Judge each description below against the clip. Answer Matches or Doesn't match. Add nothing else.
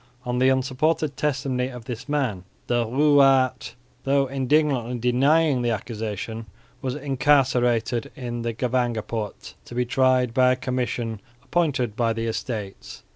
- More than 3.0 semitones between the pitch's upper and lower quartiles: Doesn't match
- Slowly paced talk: Matches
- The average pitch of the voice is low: Matches